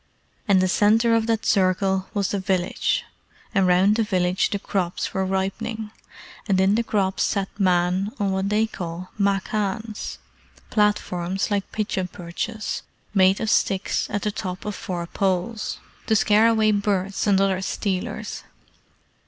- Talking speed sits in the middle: Yes, average, 150 wpm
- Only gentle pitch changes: Yes, narrow, 2.1 semitones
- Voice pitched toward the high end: Yes, high, 195 Hz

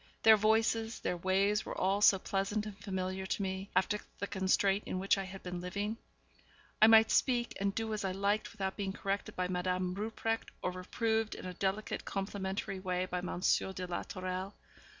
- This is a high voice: Yes, high, 195 Hz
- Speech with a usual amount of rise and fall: No, narrow, 2.2 semitones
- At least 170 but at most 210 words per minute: Yes, average, 190 wpm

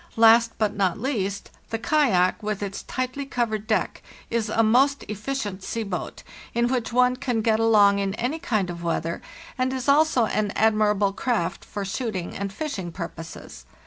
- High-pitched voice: Yes, high, 220 Hz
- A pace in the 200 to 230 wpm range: No, average, 170 wpm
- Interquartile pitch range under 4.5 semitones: Yes, average, 3.9 semitones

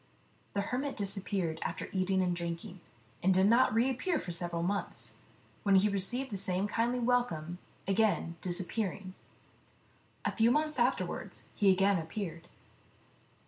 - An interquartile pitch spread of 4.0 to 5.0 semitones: Yes, average, 4.3 semitones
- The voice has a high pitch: Yes, high, 195 Hz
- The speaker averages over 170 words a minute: No, slow, 135 wpm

